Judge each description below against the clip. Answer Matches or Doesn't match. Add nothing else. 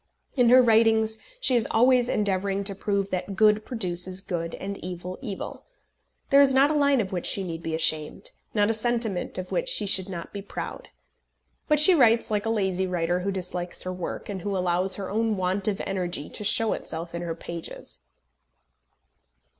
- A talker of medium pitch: Doesn't match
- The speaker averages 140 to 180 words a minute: Doesn't match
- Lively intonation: Doesn't match